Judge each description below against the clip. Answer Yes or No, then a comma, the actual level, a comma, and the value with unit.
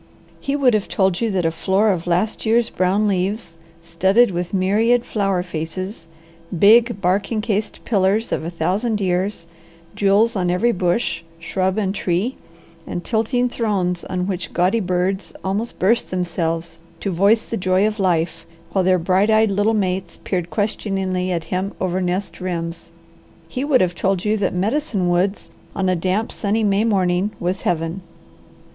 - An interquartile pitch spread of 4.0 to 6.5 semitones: No, average, 3.0 semitones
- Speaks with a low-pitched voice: No, high, 190 Hz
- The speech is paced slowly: No, average, 165 wpm